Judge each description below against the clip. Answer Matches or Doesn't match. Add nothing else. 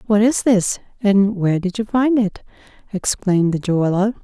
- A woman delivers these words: Matches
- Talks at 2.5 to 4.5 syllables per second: Doesn't match